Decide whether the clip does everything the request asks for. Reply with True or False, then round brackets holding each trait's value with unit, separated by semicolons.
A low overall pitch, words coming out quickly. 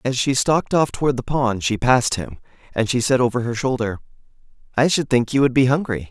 True (125 Hz; 225 wpm)